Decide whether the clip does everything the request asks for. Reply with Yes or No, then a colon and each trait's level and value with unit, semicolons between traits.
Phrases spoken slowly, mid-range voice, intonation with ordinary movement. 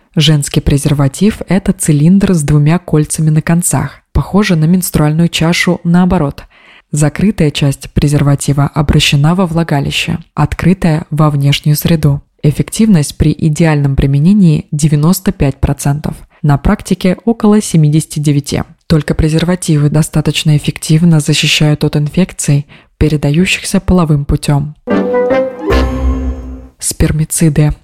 Yes: slow, 95 wpm; medium, 155 Hz; average, 3.1 semitones